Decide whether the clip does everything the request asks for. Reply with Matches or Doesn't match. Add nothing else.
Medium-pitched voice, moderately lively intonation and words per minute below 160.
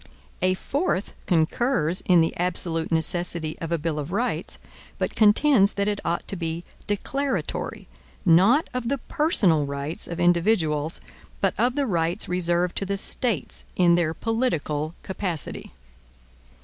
Matches